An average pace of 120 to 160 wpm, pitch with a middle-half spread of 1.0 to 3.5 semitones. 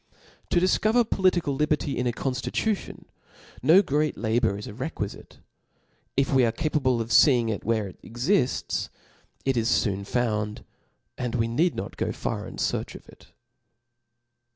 No: average, 155 wpm; average, 5.1 semitones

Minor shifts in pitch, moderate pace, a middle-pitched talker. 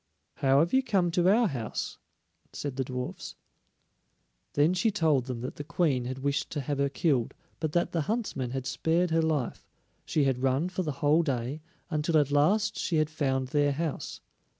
No: average, 3.9 semitones; average, 190 wpm; medium, 145 Hz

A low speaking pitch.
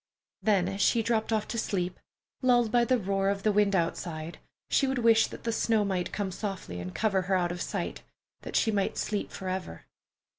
No: high, 200 Hz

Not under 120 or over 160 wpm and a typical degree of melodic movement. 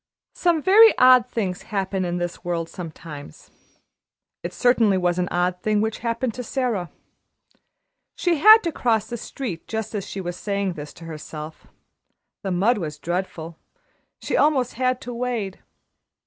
No: average, 155 wpm; wide, 5.9 semitones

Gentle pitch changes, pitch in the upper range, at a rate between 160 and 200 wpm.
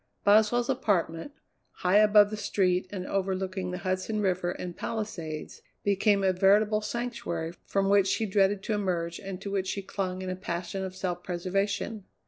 Yes: narrow, 2.1 semitones; high, 195 Hz; average, 165 wpm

